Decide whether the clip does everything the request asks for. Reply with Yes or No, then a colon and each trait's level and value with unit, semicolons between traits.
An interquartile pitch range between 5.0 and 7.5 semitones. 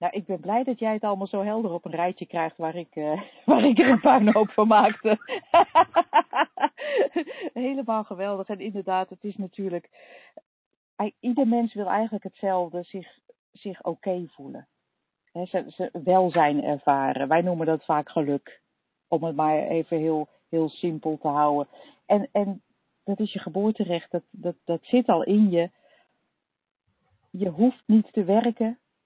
No: average, 4.3 semitones